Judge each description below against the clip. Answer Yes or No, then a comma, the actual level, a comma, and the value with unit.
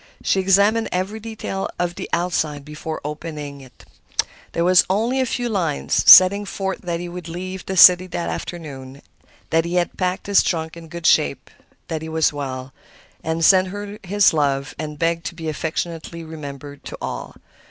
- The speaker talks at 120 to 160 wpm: No, average, 175 wpm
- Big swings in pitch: No, average, 3.6 semitones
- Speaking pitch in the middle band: Yes, medium, 170 Hz